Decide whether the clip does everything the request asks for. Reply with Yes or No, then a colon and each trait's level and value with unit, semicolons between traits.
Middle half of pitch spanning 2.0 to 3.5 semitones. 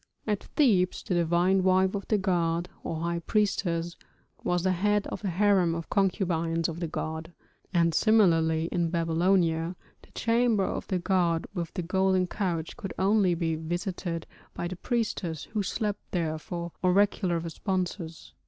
Yes: narrow, 2.6 semitones